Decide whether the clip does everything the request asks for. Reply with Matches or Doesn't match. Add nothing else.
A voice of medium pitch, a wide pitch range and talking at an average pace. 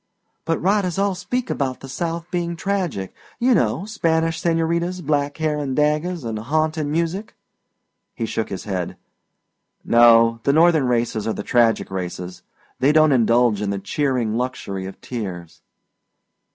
Matches